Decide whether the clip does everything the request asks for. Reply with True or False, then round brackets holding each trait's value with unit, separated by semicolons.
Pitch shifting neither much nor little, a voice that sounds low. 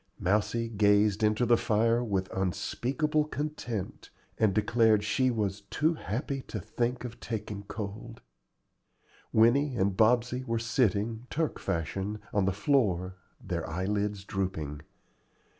True (3.5 semitones; 110 Hz)